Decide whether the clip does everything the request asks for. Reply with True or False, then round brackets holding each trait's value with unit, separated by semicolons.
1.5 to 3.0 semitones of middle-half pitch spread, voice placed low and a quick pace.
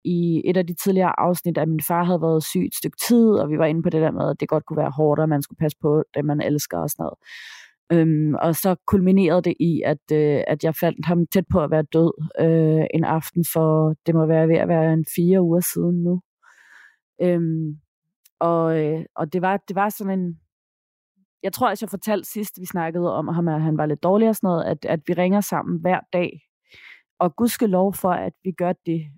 False (2.7 semitones; 170 Hz; 240 wpm)